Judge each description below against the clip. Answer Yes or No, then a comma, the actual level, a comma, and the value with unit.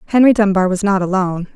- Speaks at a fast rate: No, average, 195 wpm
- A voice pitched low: No, high, 195 Hz